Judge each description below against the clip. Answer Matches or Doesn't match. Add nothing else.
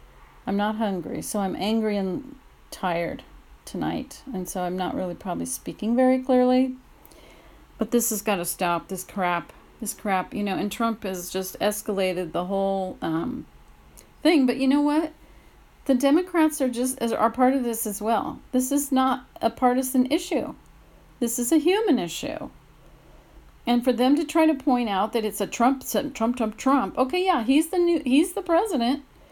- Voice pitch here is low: Doesn't match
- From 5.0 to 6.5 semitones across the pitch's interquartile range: Matches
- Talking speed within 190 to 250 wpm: Doesn't match